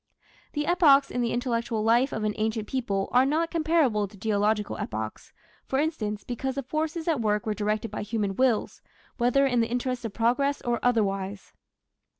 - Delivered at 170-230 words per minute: Yes, average, 175 wpm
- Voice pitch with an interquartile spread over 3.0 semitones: Yes, average, 4.3 semitones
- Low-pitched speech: No, high, 235 Hz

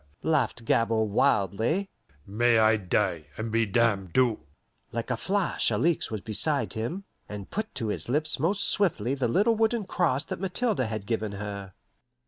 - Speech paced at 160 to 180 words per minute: Yes, average, 165 wpm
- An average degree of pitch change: No, wide, 7.3 semitones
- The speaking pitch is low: Yes, low, 115 Hz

